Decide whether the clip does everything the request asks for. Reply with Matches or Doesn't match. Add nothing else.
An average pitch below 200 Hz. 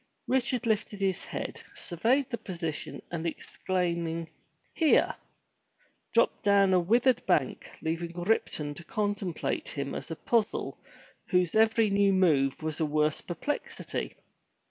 Matches